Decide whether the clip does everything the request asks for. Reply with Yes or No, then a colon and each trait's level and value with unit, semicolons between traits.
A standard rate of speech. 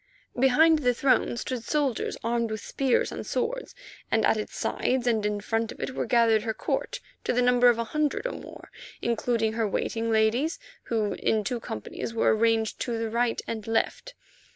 Yes: average, 190 wpm